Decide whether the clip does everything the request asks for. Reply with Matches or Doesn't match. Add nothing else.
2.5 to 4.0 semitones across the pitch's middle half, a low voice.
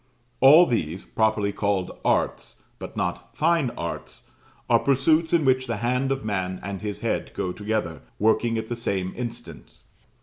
Doesn't match